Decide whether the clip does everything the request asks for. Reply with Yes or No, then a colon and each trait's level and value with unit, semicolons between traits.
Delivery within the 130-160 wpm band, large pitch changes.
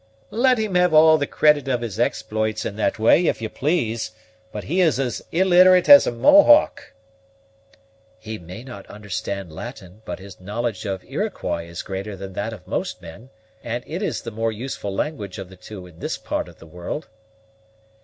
No: average, 185 wpm; wide, 7.7 semitones